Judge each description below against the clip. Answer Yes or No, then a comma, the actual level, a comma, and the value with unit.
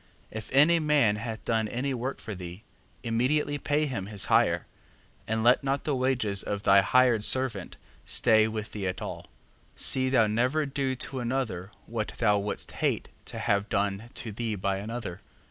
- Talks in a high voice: No, low, 115 Hz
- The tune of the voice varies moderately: Yes, average, 4.1 semitones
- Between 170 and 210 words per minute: Yes, average, 180 wpm